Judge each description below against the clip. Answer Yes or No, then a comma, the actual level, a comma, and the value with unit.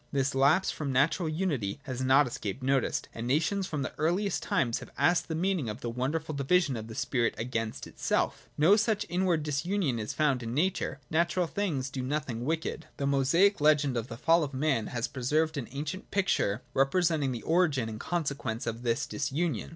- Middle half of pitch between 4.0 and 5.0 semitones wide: Yes, average, 4.6 semitones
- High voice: No, medium, 140 Hz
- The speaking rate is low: No, average, 190 wpm